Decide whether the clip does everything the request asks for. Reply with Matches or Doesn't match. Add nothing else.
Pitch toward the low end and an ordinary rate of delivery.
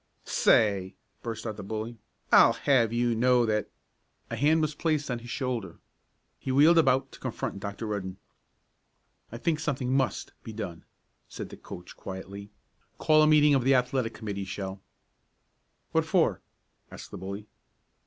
Matches